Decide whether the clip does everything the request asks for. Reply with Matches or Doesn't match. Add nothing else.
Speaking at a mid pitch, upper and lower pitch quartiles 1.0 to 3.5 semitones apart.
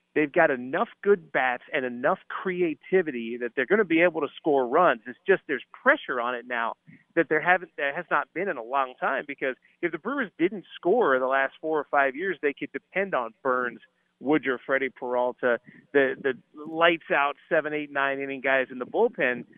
Doesn't match